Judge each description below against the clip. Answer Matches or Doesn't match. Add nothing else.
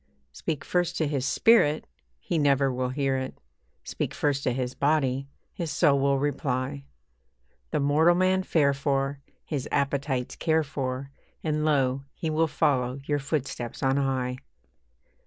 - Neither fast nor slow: Matches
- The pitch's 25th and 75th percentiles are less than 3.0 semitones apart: Matches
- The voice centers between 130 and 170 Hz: Matches